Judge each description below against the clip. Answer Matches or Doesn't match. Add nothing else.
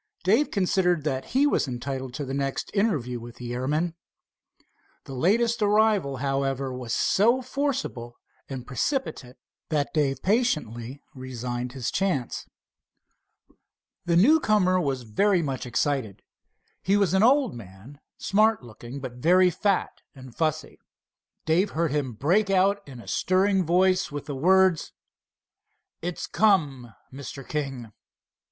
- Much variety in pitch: Matches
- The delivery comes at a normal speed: Doesn't match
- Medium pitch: Matches